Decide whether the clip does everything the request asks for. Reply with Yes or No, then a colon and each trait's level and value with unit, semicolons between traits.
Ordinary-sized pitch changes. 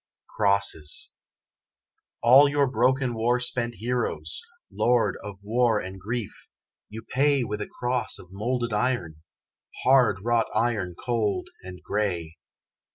Yes: average, 3.8 semitones